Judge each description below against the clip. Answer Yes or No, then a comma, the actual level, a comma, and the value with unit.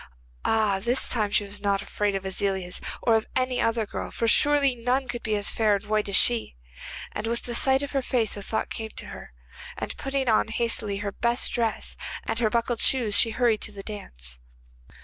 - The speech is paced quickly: Yes, fast, 215 wpm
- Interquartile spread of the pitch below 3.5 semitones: Yes, average, 2.9 semitones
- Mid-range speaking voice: No, high, 220 Hz